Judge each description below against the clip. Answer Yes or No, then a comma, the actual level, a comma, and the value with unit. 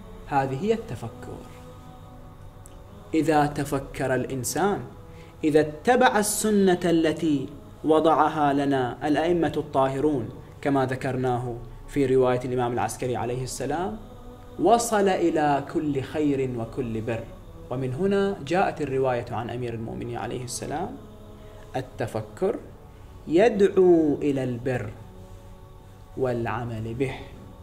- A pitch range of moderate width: Yes, average, 4.9 semitones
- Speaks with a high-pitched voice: No, low, 130 Hz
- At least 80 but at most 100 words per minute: Yes, average, 95 wpm